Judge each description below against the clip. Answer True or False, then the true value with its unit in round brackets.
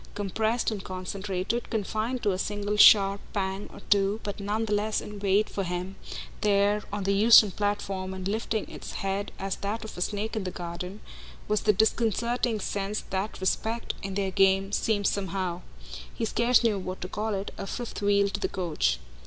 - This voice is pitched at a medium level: False (200 Hz)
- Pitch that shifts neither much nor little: False (1.9 semitones)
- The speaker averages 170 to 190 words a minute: True (185 wpm)